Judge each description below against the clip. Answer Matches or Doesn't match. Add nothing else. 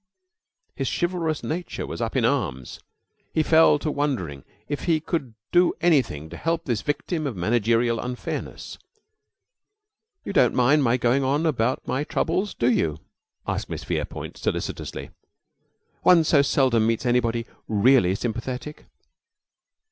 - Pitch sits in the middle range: Doesn't match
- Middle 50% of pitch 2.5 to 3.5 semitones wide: Doesn't match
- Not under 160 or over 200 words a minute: Doesn't match